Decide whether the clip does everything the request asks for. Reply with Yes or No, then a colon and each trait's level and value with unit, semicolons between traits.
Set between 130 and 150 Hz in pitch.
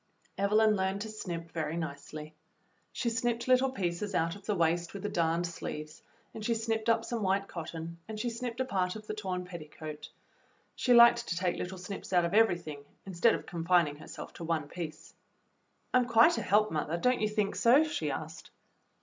No: high, 190 Hz